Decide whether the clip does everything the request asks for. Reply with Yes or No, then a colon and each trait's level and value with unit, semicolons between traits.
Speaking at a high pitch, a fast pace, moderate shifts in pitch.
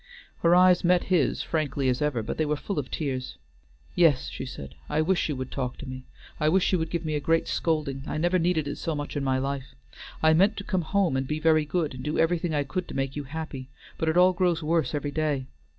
No: medium, 155 Hz; fast, 250 wpm; average, 3.8 semitones